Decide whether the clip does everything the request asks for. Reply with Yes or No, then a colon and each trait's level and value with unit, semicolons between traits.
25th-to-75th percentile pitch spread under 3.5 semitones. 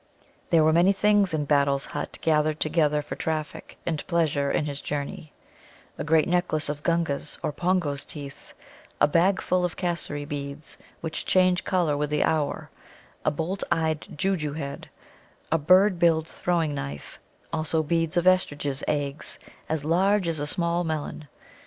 Yes: average, 2.9 semitones